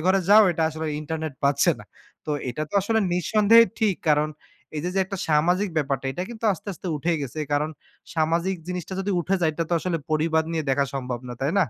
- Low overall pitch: No, medium, 160 Hz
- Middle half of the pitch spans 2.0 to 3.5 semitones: No, average, 3.9 semitones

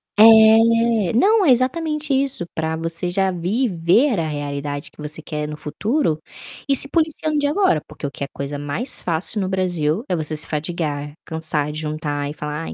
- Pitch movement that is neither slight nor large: No, wide, 7.6 semitones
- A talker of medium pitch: Yes, medium, 170 Hz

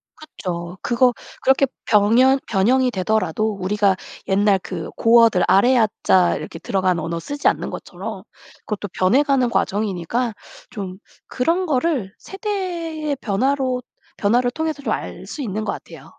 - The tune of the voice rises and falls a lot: Yes, wide, 5.7 semitones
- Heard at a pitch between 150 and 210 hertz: No, high, 230 Hz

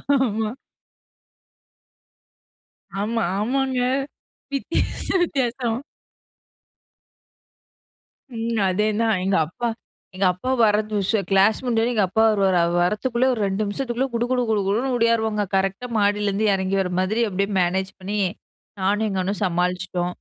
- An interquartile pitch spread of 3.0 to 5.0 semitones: Yes, average, 3.3 semitones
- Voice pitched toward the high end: Yes, high, 210 Hz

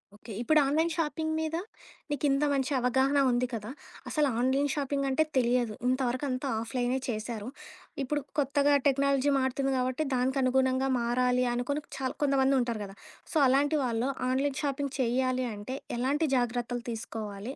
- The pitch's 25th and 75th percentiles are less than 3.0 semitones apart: Yes, narrow, 2.4 semitones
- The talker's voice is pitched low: No, very high, 260 Hz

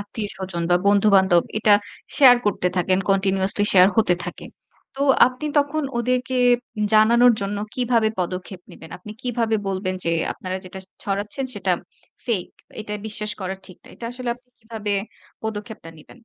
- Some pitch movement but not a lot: Yes, average, 3.8 semitones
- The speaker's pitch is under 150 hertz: No, high, 210 Hz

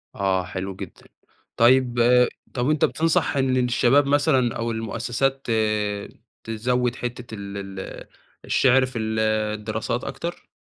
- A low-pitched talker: Yes, low, 120 Hz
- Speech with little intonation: No, average, 3.1 semitones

